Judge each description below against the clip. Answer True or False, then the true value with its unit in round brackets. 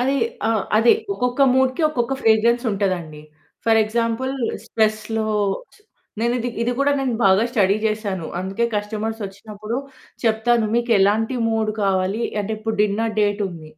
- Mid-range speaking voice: False (220 Hz)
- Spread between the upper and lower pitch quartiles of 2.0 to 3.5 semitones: True (2.5 semitones)